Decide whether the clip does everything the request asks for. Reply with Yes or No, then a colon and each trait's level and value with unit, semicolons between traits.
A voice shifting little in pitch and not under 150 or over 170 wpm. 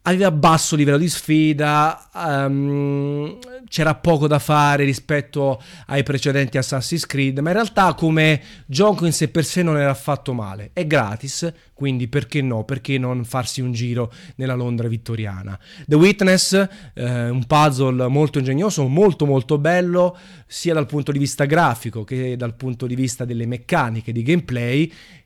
No: average, 4.1 semitones; average, 155 wpm